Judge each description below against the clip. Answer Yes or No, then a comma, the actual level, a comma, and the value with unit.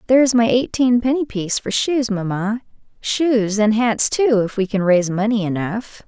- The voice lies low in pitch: No, high, 225 Hz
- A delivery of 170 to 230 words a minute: Yes, average, 180 wpm